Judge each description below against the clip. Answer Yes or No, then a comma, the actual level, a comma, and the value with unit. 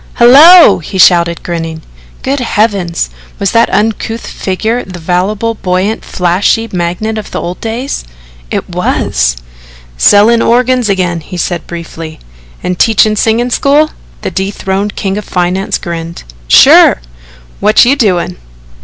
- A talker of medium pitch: No, high, 195 Hz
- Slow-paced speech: Yes, slow, 130 wpm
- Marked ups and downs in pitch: No, average, 4.6 semitones